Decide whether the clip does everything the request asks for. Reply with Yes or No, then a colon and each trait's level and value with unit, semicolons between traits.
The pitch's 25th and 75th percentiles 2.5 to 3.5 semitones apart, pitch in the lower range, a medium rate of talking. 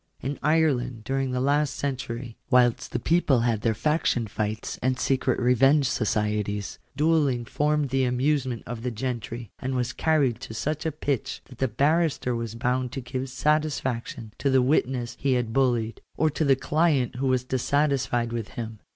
Yes: average, 3.1 semitones; low, 130 Hz; average, 175 wpm